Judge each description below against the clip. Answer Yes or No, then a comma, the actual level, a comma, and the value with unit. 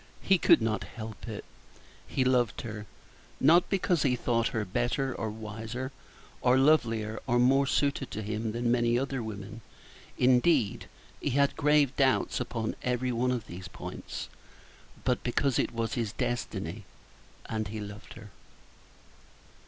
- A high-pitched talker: No, low, 120 Hz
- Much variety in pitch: No, average, 3.1 semitones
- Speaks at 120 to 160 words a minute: Yes, average, 145 wpm